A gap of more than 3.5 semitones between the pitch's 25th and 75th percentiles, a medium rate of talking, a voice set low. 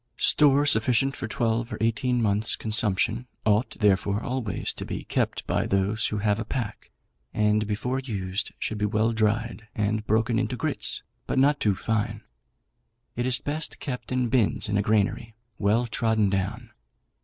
No: average, 2.7 semitones; average, 165 wpm; low, 110 Hz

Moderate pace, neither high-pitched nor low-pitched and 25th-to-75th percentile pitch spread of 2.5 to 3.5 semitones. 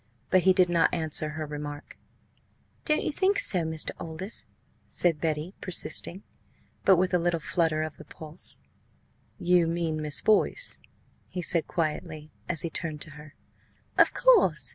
Yes: average, 155 wpm; medium, 165 Hz; average, 2.8 semitones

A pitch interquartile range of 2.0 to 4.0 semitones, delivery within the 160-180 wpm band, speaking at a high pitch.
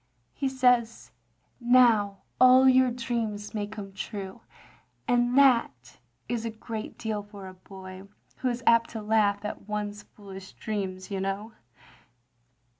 No: average, 3.3 semitones; average, 140 wpm; high, 215 Hz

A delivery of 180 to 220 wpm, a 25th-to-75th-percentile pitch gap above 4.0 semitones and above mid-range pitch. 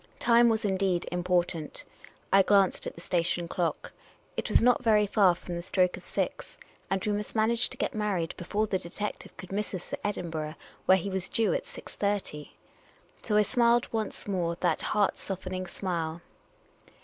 No: average, 185 wpm; average, 3.2 semitones; high, 195 Hz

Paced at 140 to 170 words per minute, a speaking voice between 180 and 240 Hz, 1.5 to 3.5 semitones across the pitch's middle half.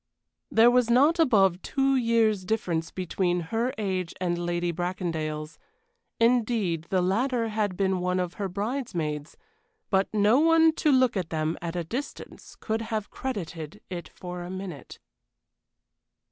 No: average, 145 wpm; high, 190 Hz; average, 4.9 semitones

